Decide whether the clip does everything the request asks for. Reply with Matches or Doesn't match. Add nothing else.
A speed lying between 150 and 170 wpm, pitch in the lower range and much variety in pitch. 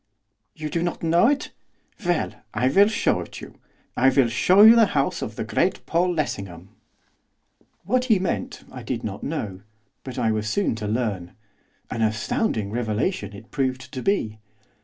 Matches